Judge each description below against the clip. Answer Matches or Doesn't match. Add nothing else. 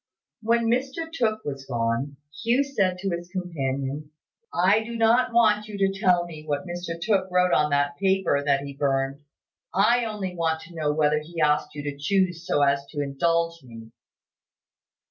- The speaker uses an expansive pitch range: Matches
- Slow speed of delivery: Doesn't match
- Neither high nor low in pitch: Matches